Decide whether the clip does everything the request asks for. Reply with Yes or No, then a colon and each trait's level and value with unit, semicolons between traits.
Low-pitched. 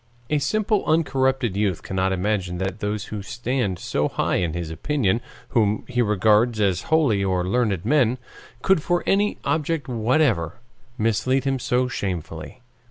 Yes: low, 110 Hz